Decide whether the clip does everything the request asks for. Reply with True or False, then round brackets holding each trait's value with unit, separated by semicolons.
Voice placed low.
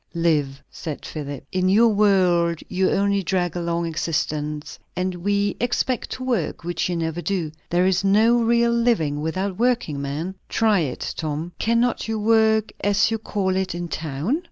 False (185 Hz)